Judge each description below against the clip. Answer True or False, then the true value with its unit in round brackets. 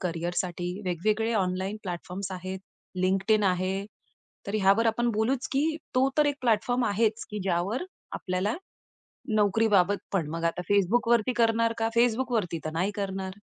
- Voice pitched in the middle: False (200 Hz)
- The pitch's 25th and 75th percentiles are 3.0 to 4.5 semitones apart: True (3.6 semitones)